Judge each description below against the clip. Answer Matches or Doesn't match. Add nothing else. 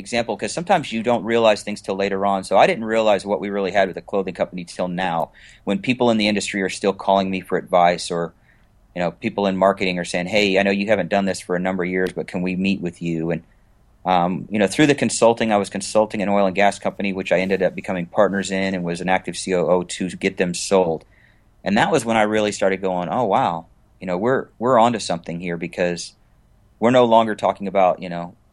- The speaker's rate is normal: Doesn't match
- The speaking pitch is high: Doesn't match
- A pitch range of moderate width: Matches